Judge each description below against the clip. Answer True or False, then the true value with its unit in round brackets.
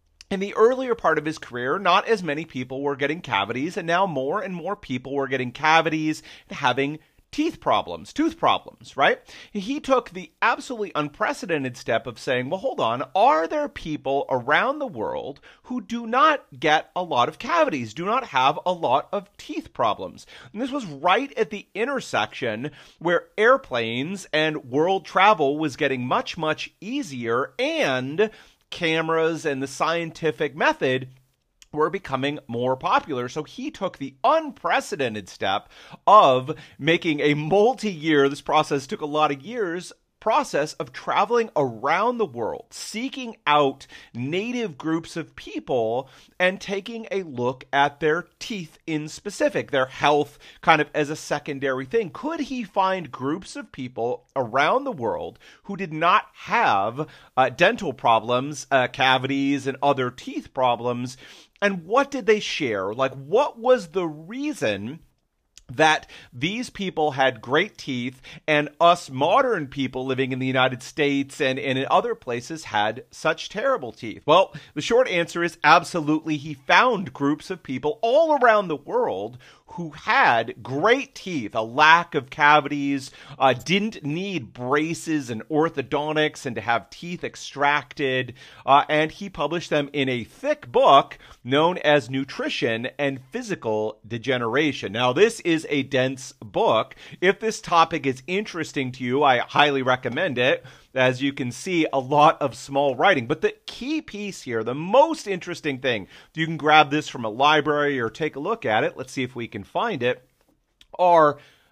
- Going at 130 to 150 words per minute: False (160 wpm)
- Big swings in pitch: True (6.5 semitones)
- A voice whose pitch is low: False (155 Hz)